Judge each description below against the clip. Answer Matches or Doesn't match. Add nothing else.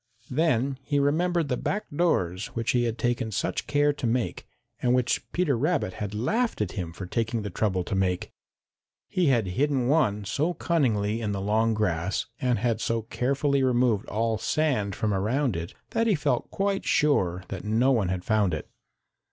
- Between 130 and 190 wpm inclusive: Matches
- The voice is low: Matches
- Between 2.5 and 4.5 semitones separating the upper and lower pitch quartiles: Doesn't match